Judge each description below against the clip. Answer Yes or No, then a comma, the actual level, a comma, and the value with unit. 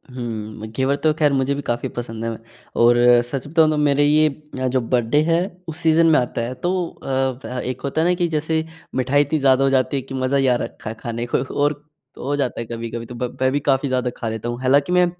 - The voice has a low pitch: Yes, low, 130 Hz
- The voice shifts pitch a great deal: No, average, 3.3 semitones